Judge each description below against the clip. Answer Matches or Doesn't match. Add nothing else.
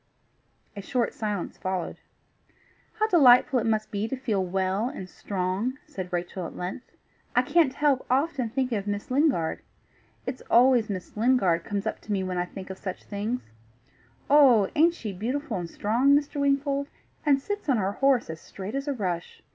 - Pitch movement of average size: Doesn't match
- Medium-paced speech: Matches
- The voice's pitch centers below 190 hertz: Doesn't match